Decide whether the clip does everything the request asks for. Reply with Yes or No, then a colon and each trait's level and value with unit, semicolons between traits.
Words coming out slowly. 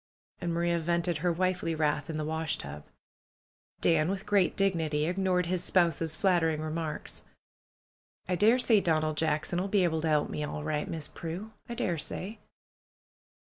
No: average, 155 wpm